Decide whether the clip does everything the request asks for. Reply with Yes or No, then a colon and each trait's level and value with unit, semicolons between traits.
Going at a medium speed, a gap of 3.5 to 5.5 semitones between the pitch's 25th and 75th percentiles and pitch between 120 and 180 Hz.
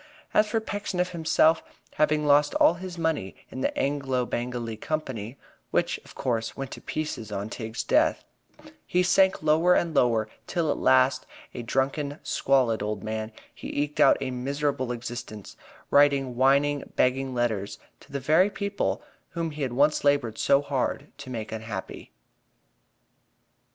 Yes: average, 150 wpm; average, 4.2 semitones; low, 135 Hz